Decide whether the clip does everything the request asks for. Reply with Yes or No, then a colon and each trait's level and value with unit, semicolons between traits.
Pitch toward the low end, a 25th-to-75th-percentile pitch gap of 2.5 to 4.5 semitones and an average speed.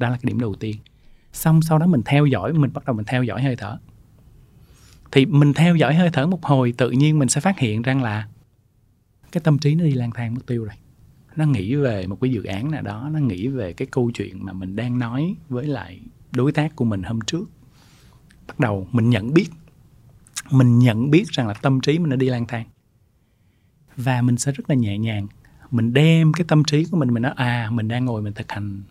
Yes: low, 125 Hz; average, 3.8 semitones; average, 235 wpm